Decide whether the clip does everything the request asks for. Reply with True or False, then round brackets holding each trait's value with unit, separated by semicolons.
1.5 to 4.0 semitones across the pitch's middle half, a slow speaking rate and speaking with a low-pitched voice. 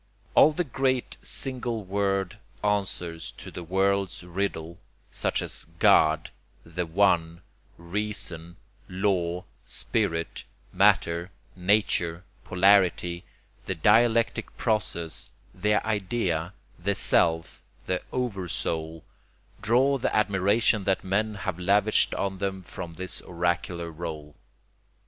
True (3.3 semitones; 105 wpm; 95 Hz)